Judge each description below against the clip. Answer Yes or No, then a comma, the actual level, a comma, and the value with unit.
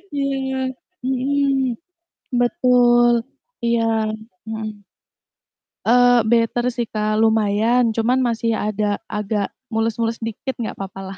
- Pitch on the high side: Yes, high, 230 Hz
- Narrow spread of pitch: Yes, narrow, 2.3 semitones